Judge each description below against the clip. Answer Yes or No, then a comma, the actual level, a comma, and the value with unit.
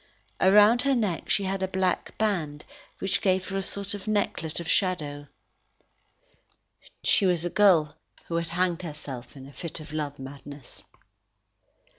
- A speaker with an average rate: Yes, average, 155 wpm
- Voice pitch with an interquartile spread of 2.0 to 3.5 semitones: No, average, 4.6 semitones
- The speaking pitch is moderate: Yes, medium, 175 Hz